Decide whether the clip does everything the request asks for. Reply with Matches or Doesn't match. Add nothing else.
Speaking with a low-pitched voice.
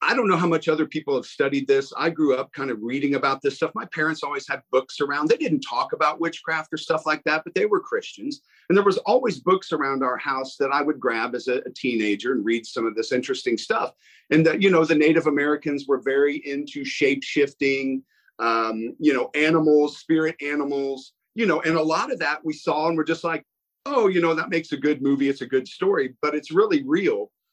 Doesn't match